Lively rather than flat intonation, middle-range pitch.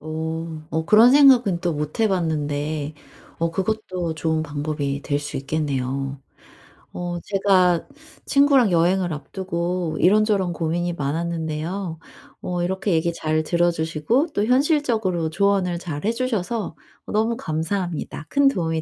No: average, 4.1 semitones; medium, 170 Hz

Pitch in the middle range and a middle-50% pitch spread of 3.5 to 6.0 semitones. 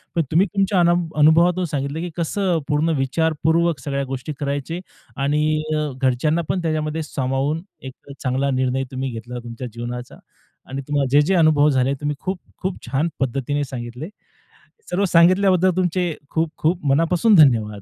Yes: medium, 150 Hz; average, 4.0 semitones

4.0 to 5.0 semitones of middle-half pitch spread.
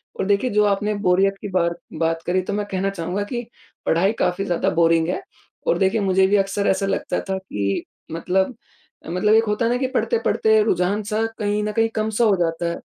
No: average, 2.9 semitones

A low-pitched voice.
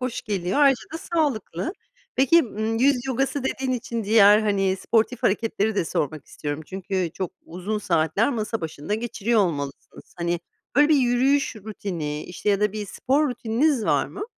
No: high, 215 Hz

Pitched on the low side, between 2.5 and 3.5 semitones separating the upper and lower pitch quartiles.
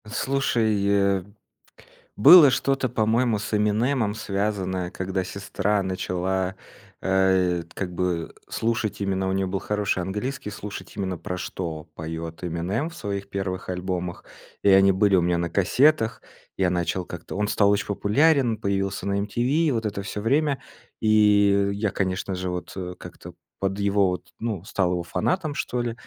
Yes: low, 100 Hz; average, 2.8 semitones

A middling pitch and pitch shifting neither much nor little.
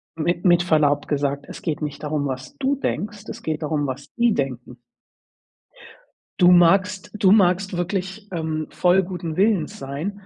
Yes: medium, 175 Hz; average, 4.5 semitones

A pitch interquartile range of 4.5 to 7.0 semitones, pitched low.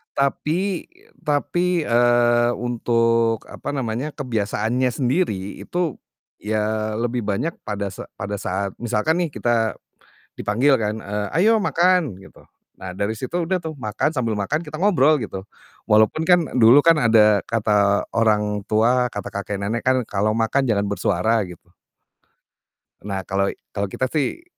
Yes: wide, 5.4 semitones; low, 115 Hz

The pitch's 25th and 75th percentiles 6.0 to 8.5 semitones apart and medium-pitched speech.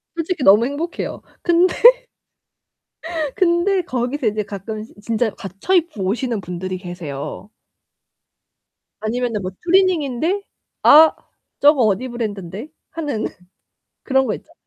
No: wide, 7.9 semitones; high, 245 Hz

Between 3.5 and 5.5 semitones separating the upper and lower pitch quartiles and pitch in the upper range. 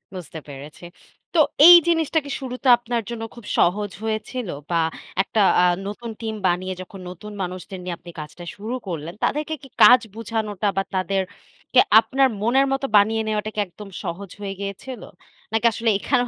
Yes: average, 4.6 semitones; high, 210 Hz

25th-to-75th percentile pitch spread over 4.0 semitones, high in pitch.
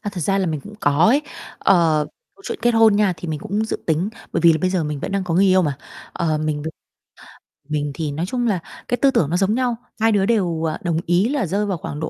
No: average, 5.0 semitones; medium, 180 Hz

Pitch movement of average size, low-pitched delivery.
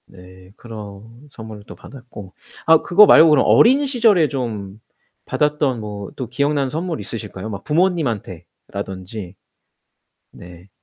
No: wide, 7.0 semitones; low, 115 Hz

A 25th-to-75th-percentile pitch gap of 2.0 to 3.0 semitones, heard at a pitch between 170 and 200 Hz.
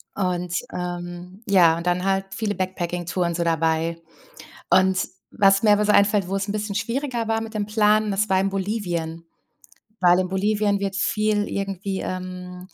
Yes: narrow, 2.6 semitones; high, 190 Hz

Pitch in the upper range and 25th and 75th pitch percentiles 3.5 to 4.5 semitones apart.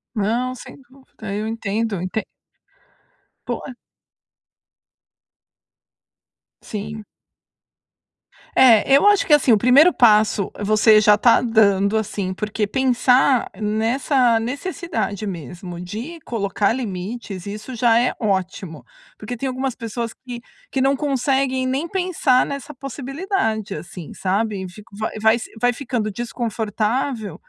Yes: high, 225 Hz; average, 3.8 semitones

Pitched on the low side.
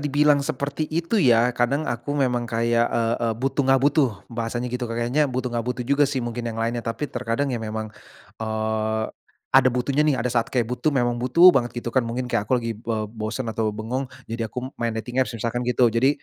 Yes: low, 120 Hz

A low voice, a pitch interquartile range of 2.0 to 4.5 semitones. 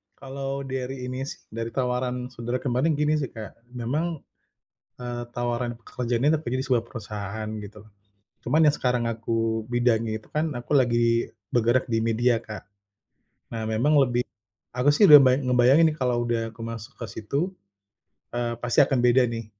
Yes: low, 120 Hz; narrow, 2.5 semitones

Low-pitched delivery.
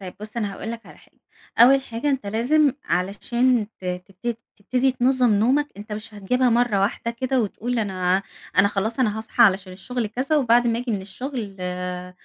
No: high, 225 Hz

